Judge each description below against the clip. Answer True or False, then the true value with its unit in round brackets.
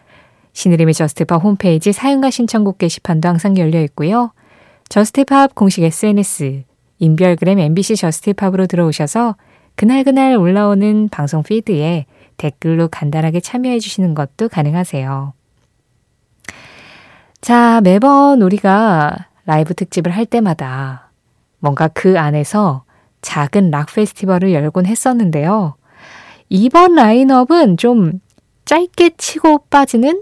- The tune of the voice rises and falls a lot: True (6.4 semitones)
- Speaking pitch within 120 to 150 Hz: False (185 Hz)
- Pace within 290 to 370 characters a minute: False (280 characters per minute)